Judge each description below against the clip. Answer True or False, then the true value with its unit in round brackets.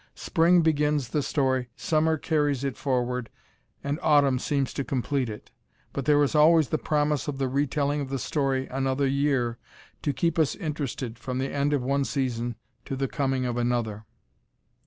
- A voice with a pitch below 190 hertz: True (140 Hz)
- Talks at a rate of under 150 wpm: False (175 wpm)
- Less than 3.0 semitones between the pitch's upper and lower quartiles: True (2.5 semitones)